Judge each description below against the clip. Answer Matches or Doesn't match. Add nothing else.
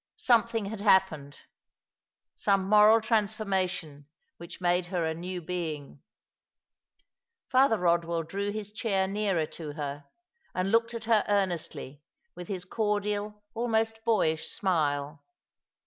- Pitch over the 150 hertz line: Matches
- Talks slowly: Matches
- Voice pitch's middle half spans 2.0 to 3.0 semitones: Doesn't match